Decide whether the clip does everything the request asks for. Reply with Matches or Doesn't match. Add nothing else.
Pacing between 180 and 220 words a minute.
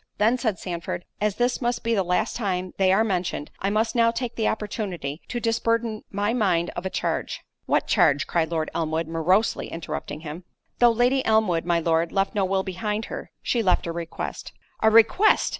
Matches